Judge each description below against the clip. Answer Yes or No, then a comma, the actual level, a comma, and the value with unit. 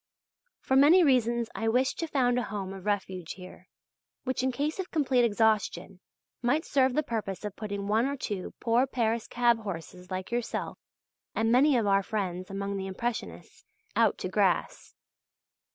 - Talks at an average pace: Yes, average, 170 wpm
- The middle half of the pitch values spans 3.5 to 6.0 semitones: Yes, average, 4.6 semitones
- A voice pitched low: No, high, 225 Hz